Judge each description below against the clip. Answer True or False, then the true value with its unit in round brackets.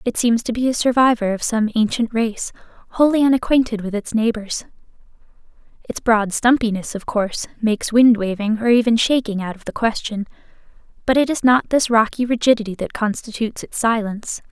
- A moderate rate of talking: True (170 wpm)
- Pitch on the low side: False (230 Hz)